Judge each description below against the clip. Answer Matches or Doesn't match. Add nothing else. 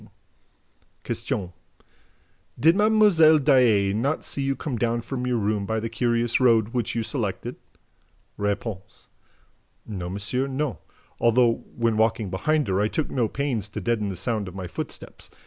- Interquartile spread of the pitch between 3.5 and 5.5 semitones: Matches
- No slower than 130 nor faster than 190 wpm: Matches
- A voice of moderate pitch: Doesn't match